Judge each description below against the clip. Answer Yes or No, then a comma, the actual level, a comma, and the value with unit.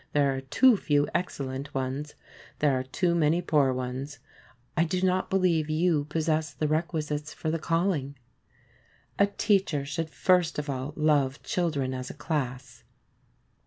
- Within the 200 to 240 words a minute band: No, average, 150 wpm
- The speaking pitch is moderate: Yes, medium, 150 Hz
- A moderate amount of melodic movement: Yes, average, 3.4 semitones